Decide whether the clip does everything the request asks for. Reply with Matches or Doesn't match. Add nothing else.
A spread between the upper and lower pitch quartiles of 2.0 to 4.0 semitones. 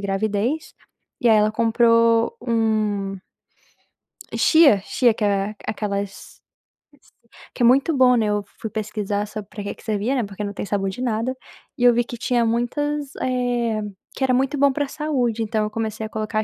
Matches